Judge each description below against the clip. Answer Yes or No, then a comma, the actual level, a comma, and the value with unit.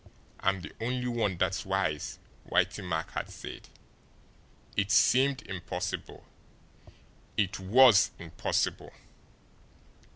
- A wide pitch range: No, average, 4.7 semitones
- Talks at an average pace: No, slow, 95 wpm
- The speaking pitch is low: Yes, very low, 95 Hz